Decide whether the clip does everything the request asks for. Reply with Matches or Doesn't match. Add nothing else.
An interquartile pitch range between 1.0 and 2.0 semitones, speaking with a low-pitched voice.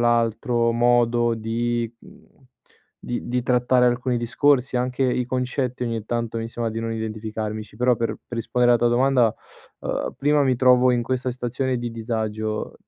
Matches